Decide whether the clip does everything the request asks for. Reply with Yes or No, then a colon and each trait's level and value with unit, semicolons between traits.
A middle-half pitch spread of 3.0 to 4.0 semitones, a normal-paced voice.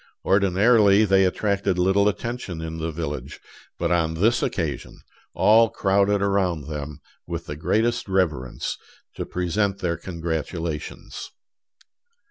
No: average, 3.7 semitones; slow, 115 wpm